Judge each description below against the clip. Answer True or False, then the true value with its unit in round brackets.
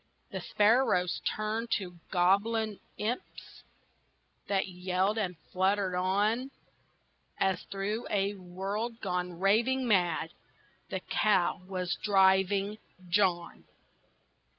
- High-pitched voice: True (195 Hz)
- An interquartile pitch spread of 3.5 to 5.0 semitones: False (2.7 semitones)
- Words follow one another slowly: True (95 wpm)